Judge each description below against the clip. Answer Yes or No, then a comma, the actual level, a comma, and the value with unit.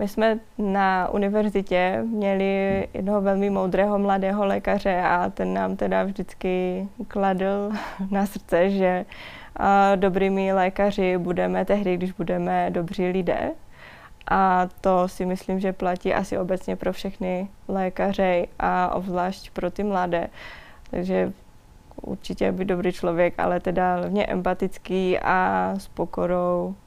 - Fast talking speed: No, average, 125 wpm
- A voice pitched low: No, medium, 185 Hz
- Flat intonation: Yes, narrow, 1.6 semitones